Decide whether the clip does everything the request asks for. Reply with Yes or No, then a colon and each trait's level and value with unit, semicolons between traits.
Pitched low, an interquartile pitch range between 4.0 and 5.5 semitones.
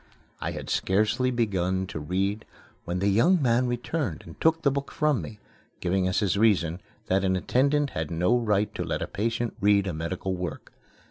Yes: low, 100 Hz; average, 4.9 semitones